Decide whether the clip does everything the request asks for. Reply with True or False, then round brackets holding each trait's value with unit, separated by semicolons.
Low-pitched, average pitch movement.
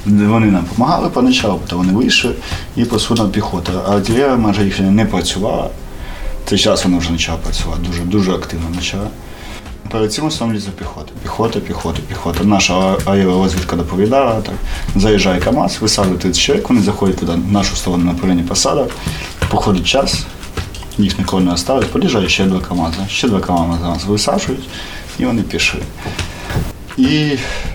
True (95 Hz; 3.2 semitones)